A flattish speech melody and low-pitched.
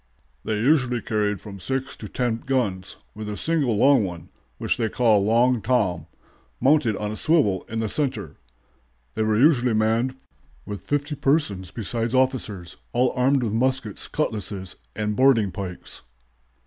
No: average, 4.0 semitones; low, 115 Hz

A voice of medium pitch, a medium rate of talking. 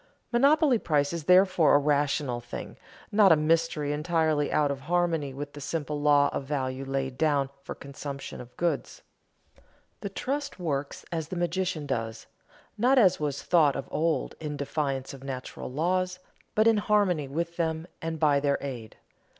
Yes: medium, 150 Hz; average, 160 wpm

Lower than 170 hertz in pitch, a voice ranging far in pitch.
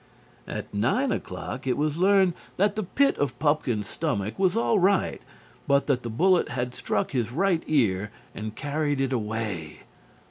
Yes: medium, 140 Hz; wide, 8.0 semitones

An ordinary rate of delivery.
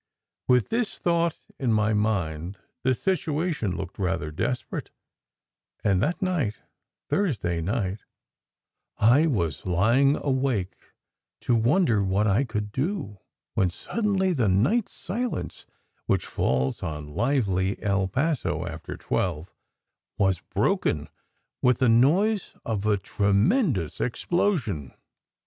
No: slow, 115 wpm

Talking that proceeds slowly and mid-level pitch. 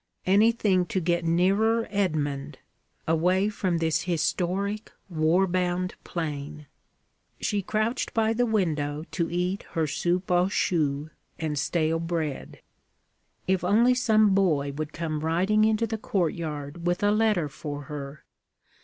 Yes: slow, 130 wpm; medium, 175 Hz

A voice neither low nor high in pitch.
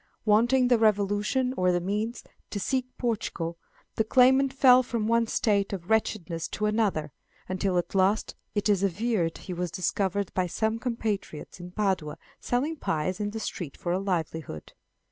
No: high, 205 Hz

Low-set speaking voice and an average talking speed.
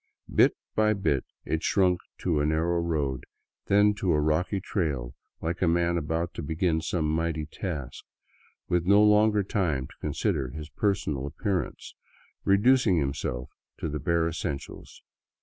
Yes: very low, 85 Hz; average, 150 wpm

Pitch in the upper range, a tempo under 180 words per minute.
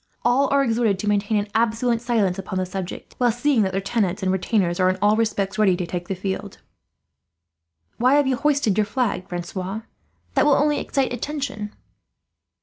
No: high, 215 Hz; average, 185 wpm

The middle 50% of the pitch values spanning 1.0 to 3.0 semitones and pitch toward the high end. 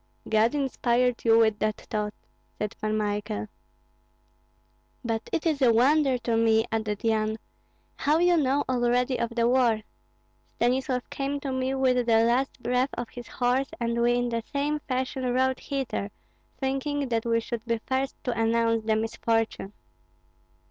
Yes: average, 2.7 semitones; high, 240 Hz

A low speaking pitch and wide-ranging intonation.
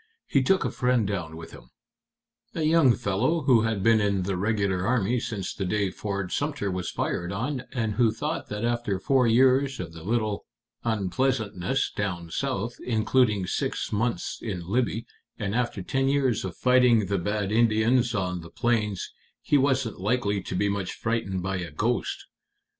No: low, 110 Hz; average, 4.4 semitones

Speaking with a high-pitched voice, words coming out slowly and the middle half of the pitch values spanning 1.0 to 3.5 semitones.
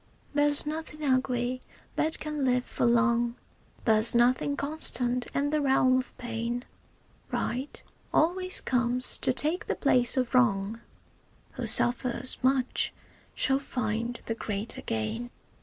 Yes: very high, 250 Hz; slow, 125 wpm; average, 2.9 semitones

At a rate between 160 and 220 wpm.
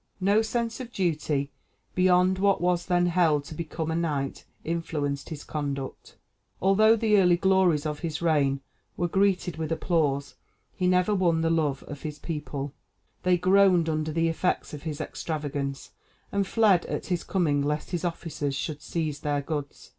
Yes: average, 165 wpm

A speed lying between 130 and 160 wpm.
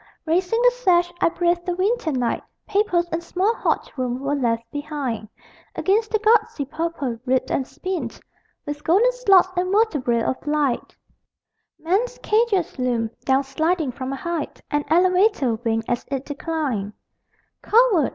Yes: average, 150 wpm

